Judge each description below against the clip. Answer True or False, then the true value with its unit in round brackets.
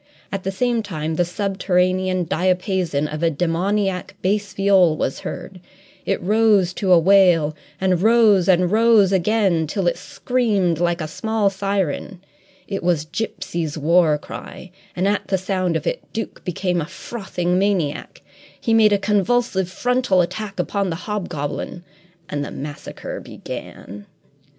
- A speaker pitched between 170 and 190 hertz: True (185 Hz)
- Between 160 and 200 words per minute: False (145 wpm)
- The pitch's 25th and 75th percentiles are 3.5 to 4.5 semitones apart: False (3.0 semitones)